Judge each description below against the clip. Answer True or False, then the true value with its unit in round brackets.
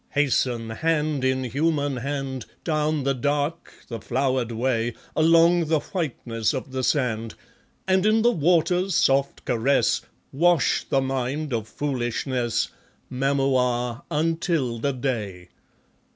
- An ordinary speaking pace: False (120 wpm)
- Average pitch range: True (4.1 semitones)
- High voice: False (135 Hz)